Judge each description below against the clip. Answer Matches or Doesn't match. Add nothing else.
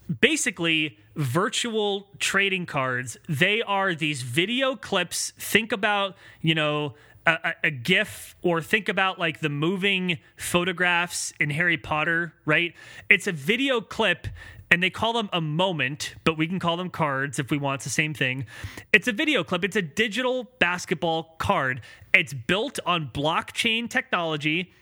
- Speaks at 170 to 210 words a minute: Doesn't match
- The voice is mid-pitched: Matches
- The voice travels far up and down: Doesn't match